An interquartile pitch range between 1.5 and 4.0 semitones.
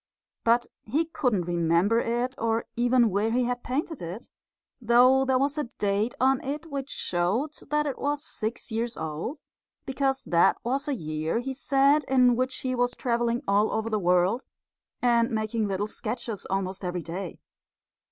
No: average, 4.7 semitones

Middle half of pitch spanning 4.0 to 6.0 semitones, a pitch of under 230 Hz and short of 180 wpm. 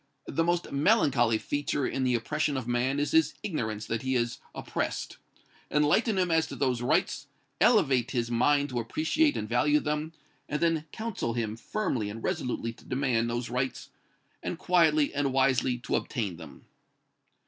Yes: average, 4.4 semitones; low, 135 Hz; average, 165 wpm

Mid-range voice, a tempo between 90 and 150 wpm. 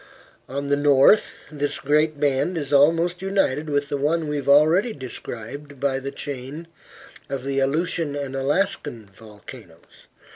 Yes: medium, 145 Hz; average, 145 wpm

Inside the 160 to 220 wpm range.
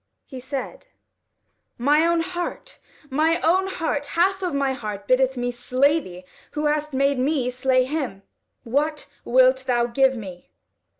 No: average, 145 wpm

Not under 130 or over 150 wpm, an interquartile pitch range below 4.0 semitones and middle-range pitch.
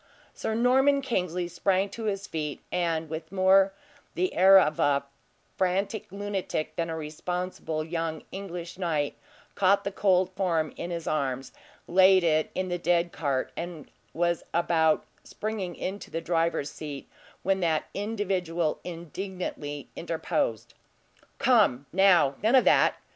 Yes: slow, 135 wpm; average, 3.2 semitones; medium, 175 Hz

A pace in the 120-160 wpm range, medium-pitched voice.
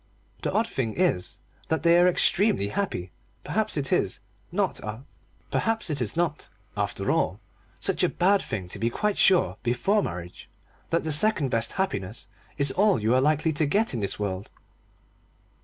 Yes: average, 155 wpm; medium, 145 Hz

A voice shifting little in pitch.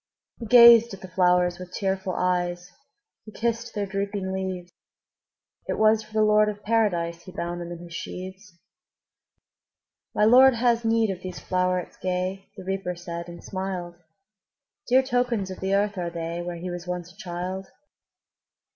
No: average, 3.1 semitones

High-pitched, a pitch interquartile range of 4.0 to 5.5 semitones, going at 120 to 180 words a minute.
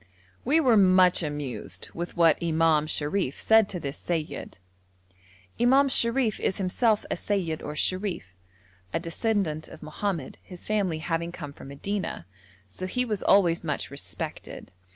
No: medium, 175 Hz; average, 5.0 semitones; average, 145 wpm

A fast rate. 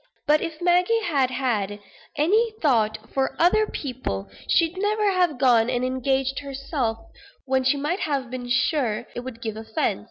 No: average, 160 wpm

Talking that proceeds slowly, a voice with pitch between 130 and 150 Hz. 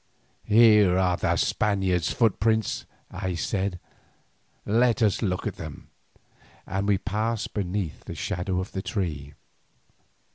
No: slow, 120 wpm; low, 100 Hz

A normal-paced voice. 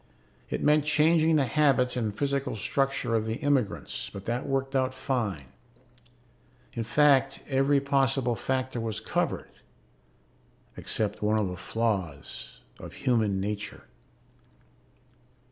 No: slow, 120 wpm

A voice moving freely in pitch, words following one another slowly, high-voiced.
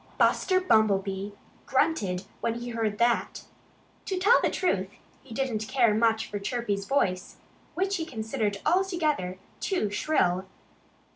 Yes: wide, 7.1 semitones; slow, 130 wpm; high, 225 Hz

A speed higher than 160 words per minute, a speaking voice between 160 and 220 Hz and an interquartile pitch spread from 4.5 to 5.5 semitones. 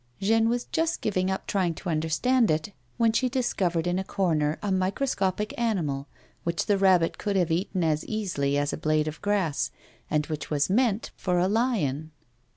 Yes: average, 180 wpm; medium, 185 Hz; average, 5.1 semitones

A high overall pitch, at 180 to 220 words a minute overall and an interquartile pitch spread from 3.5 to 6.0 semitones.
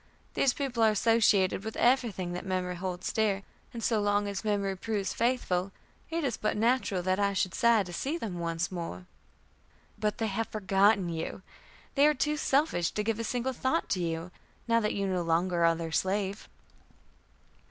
Yes: high, 205 Hz; average, 185 wpm; average, 4.0 semitones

